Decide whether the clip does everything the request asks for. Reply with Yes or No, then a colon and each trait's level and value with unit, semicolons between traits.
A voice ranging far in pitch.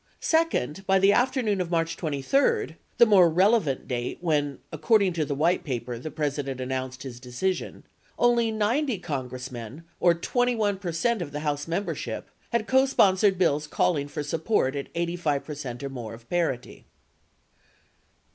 Yes: wide, 6.6 semitones